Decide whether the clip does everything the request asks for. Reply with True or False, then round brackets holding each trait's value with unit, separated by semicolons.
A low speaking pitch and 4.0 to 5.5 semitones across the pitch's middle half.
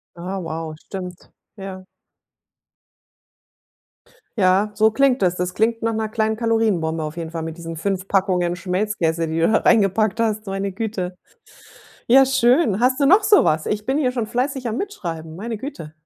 False (200 Hz; 4.6 semitones)